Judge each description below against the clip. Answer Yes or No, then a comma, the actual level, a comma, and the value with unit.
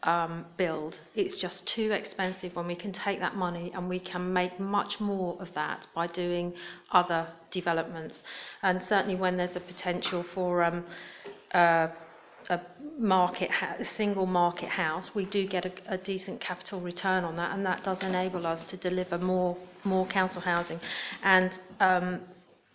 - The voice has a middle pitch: Yes, medium, 180 Hz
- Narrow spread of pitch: Yes, narrow, 1.5 semitones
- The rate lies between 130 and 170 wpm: Yes, average, 165 wpm